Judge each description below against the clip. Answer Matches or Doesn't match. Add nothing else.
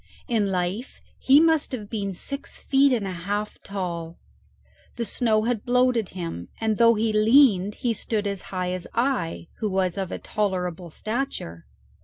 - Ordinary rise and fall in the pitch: Matches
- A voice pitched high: Matches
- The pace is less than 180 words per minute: Matches